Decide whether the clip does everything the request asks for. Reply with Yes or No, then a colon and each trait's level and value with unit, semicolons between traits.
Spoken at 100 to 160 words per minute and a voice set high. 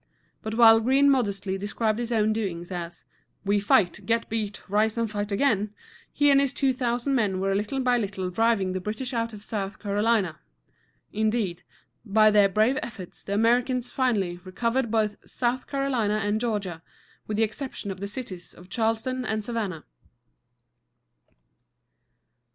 Yes: average, 155 wpm; high, 215 Hz